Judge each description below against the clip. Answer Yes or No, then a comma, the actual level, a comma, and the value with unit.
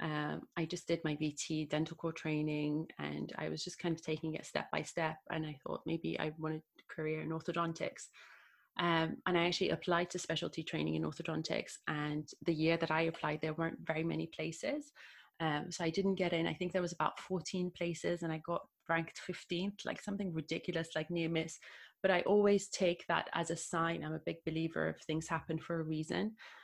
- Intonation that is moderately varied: No, narrow, 1.9 semitones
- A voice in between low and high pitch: Yes, medium, 165 Hz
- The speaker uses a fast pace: Yes, fast, 210 wpm